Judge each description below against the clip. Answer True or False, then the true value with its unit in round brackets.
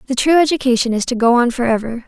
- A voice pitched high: True (250 Hz)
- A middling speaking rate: False (230 wpm)